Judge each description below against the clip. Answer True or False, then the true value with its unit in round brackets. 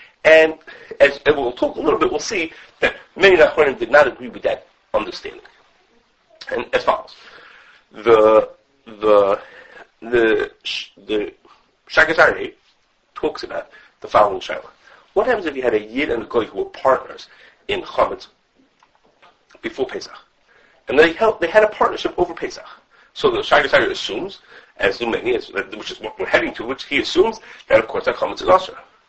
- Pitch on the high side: True (370 Hz)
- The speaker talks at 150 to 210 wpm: True (165 wpm)